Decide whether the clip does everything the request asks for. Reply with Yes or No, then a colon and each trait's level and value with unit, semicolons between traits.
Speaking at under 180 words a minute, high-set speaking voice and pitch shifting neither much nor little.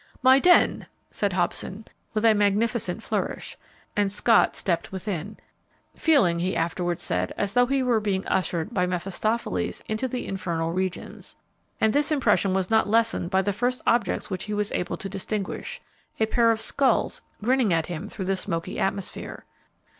Yes: average, 165 wpm; high, 205 Hz; average, 3.8 semitones